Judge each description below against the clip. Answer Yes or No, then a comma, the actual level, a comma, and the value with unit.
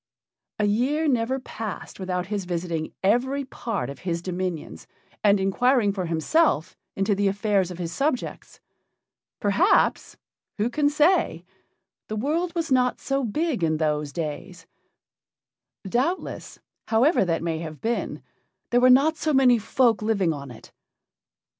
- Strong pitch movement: Yes, wide, 6.9 semitones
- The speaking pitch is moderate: No, high, 210 Hz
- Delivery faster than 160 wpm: No, average, 140 wpm